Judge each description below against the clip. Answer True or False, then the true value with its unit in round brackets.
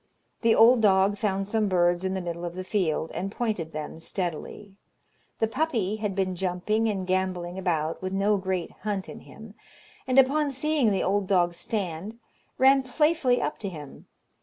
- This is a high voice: True (195 Hz)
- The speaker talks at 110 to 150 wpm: False (175 wpm)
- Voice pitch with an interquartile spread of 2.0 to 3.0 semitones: False (3.7 semitones)